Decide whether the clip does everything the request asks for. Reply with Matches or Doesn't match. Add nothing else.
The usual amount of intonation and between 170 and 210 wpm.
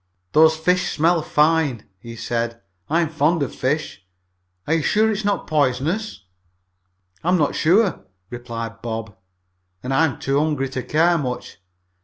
Doesn't match